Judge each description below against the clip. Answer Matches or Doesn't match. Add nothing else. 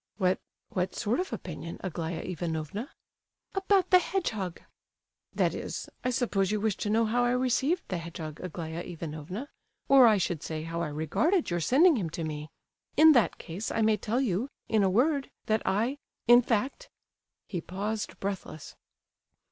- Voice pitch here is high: Matches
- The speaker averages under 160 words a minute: Matches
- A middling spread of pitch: Doesn't match